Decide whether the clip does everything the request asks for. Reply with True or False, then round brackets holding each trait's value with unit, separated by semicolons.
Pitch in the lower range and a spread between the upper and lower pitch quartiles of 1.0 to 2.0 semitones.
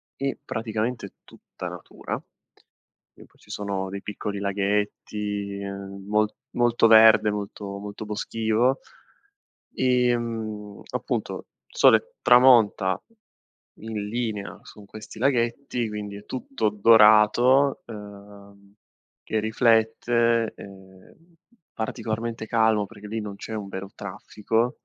False (110 Hz; 2.4 semitones)